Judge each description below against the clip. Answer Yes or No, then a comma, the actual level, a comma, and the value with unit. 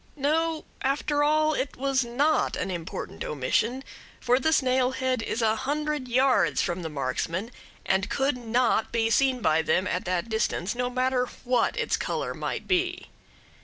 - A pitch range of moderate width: Yes, average, 4.0 semitones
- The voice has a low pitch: No, very high, 250 Hz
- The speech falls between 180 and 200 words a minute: No, average, 165 wpm